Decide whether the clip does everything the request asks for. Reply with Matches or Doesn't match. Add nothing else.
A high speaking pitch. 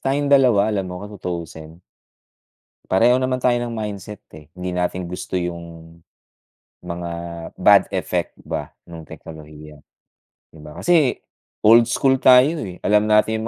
Doesn't match